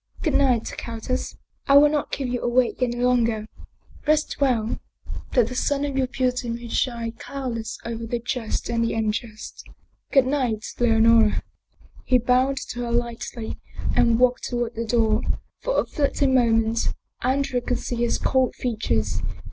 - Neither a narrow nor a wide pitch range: No, narrow, 2.1 semitones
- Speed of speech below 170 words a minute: Yes, average, 160 wpm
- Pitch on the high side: Yes, high, 240 Hz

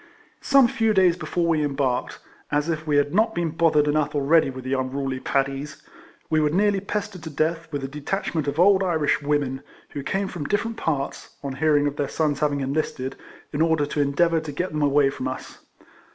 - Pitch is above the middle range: No, medium, 150 Hz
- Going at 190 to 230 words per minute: Yes, fast, 205 wpm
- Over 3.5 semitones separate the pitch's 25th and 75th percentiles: No, average, 3.1 semitones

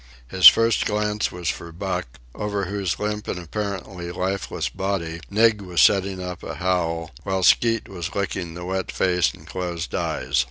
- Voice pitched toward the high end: No, very low, 95 Hz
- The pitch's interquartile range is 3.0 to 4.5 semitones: No, narrow, 2.5 semitones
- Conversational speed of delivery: Yes, average, 165 wpm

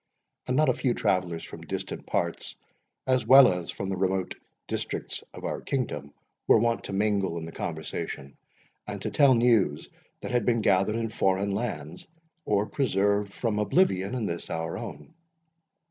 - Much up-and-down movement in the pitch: No, average, 4.6 semitones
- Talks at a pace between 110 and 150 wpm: No, average, 165 wpm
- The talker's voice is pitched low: Yes, low, 100 Hz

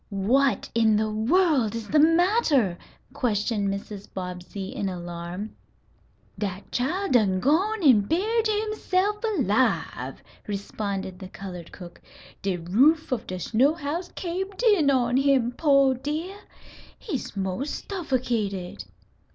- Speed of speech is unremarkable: No, slow, 120 wpm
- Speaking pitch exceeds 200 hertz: Yes, high, 245 Hz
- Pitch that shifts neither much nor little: No, wide, 8.7 semitones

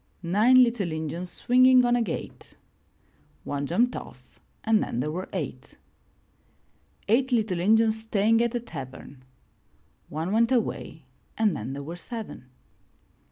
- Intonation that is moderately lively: No, wide, 6.7 semitones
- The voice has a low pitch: No, high, 215 Hz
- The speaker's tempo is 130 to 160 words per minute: Yes, average, 145 wpm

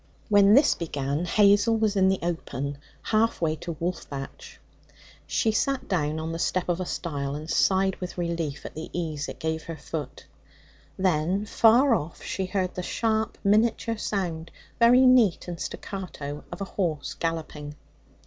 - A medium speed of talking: Yes, average, 160 wpm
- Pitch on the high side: No, medium, 175 Hz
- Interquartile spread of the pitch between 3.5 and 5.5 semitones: Yes, average, 4.6 semitones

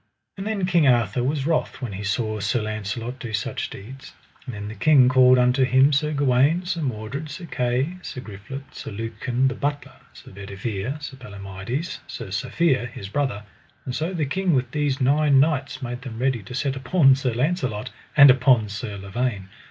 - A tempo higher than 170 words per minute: Yes, average, 185 wpm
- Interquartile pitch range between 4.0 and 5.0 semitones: Yes, average, 4.4 semitones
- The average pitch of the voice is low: Yes, low, 130 Hz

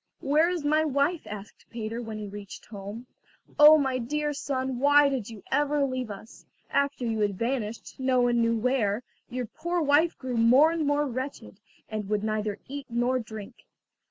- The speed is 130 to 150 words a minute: No, average, 180 wpm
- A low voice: No, very high, 255 Hz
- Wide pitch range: No, average, 4.6 semitones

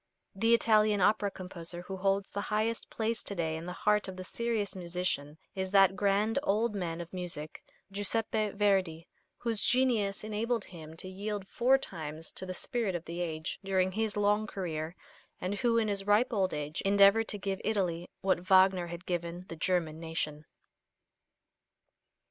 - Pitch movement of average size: Yes, average, 3.4 semitones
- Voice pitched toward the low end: No, high, 195 Hz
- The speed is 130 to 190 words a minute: Yes, average, 170 wpm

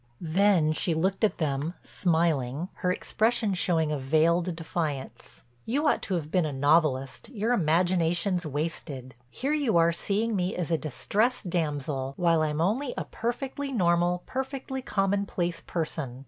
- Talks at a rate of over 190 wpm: No, average, 145 wpm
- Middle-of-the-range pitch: Yes, medium, 170 Hz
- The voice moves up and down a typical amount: Yes, average, 4.6 semitones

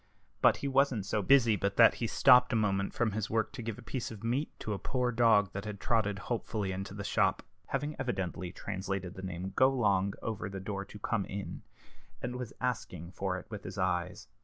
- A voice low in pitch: Yes, low, 105 Hz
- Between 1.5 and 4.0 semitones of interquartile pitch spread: Yes, average, 3.7 semitones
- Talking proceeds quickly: Yes, fast, 210 wpm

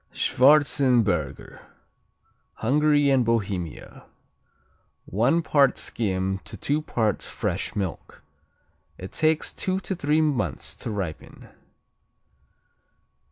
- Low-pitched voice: Yes, low, 125 Hz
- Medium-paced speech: No, slow, 90 wpm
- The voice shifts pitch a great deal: Yes, wide, 7.4 semitones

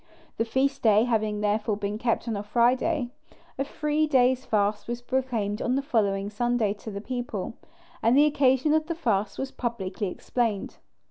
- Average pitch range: Yes, average, 3.9 semitones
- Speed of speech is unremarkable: Yes, average, 175 wpm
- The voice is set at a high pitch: Yes, high, 235 Hz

